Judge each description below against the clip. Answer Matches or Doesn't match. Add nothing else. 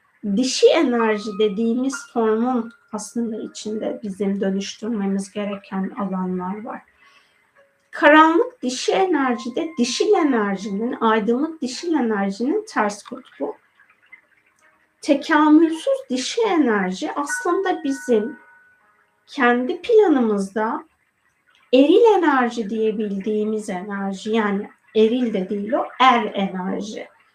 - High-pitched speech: Matches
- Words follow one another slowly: Matches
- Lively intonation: Matches